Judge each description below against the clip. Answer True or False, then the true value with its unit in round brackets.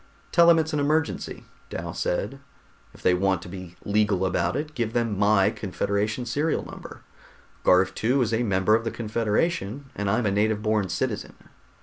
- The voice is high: False (110 Hz)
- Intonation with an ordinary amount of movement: True (4.0 semitones)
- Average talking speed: True (180 wpm)